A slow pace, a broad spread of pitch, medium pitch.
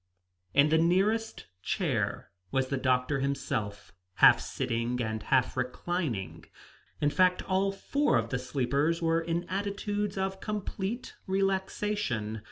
Yes: slow, 125 wpm; wide, 7.4 semitones; medium, 165 Hz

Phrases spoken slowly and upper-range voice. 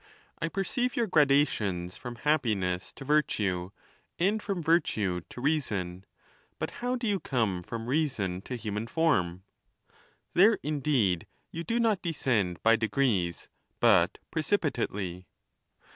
No: slow, 130 wpm; low, 125 Hz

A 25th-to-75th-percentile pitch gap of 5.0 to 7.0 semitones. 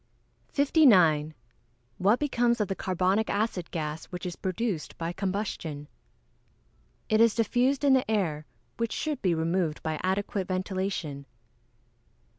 Yes: wide, 5.5 semitones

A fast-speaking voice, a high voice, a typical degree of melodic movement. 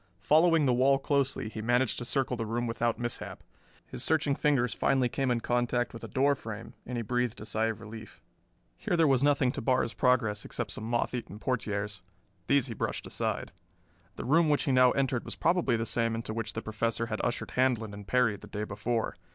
No: fast, 215 wpm; low, 120 Hz; average, 3.0 semitones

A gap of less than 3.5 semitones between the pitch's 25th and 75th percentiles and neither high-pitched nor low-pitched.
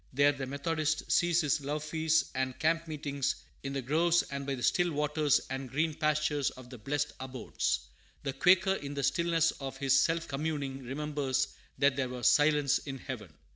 Yes: narrow, 2.6 semitones; medium, 145 Hz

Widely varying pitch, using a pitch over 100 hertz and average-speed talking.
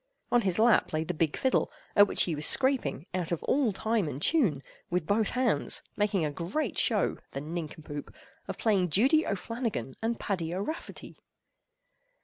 Yes: wide, 6.5 semitones; high, 190 Hz; average, 165 wpm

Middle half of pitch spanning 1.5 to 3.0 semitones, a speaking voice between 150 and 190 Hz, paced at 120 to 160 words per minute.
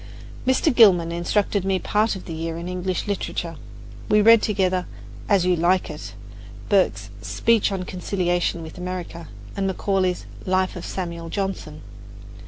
Yes: narrow, 2.4 semitones; medium, 185 Hz; average, 145 wpm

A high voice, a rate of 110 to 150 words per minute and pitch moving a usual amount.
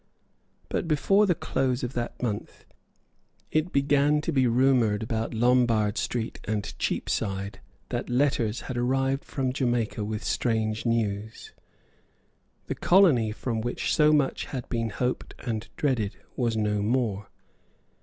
No: low, 120 Hz; slow, 135 wpm; average, 3.5 semitones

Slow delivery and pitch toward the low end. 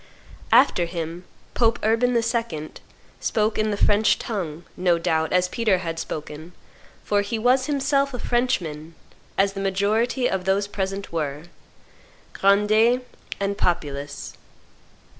No: slow, 125 wpm; high, 200 Hz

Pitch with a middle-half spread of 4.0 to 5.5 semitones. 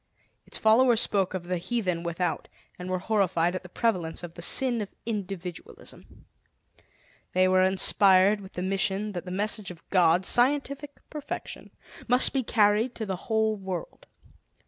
No: average, 3.5 semitones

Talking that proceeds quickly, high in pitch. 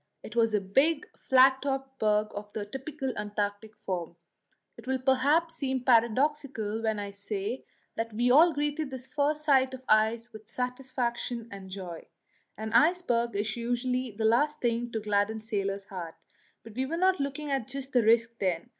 No: average, 175 wpm; high, 235 Hz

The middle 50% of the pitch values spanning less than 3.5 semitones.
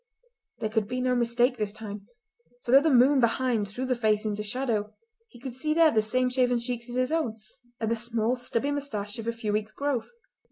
Yes: average, 2.8 semitones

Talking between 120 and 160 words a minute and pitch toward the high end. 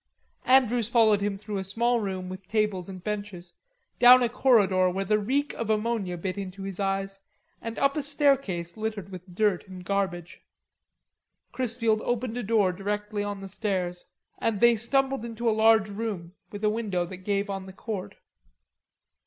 No: average, 170 wpm; high, 205 Hz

